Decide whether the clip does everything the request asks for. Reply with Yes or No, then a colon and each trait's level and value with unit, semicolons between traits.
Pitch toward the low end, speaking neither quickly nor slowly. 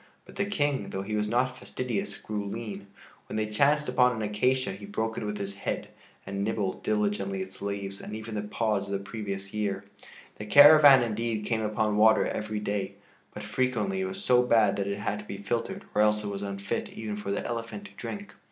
No: low, 105 Hz; fast, 215 wpm